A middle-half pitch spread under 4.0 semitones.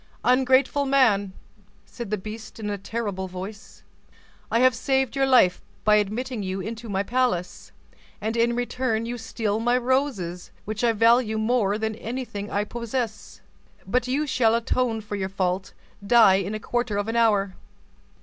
Yes: average, 3.4 semitones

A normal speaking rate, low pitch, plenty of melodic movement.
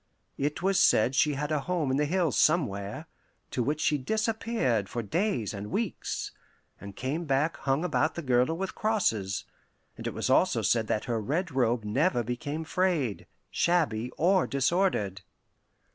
No: average, 160 wpm; medium, 145 Hz; wide, 6.5 semitones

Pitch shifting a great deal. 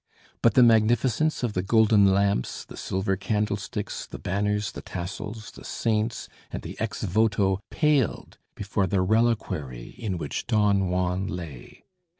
No: average, 2.7 semitones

